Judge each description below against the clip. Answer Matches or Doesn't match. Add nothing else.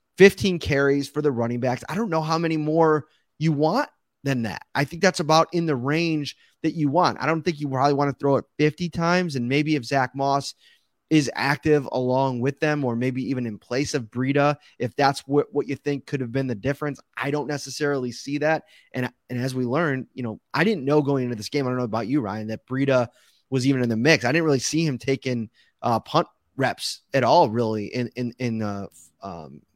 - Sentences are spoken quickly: Matches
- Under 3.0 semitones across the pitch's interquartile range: Doesn't match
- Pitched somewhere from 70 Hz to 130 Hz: Doesn't match